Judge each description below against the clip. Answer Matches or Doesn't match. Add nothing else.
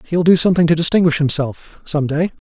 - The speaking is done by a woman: Doesn't match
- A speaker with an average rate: Matches